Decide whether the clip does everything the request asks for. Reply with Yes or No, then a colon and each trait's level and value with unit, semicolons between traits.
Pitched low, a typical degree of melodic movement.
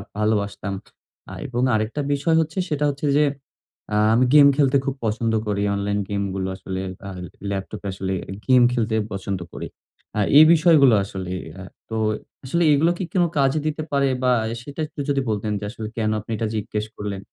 No: low, 115 Hz; wide, 5.9 semitones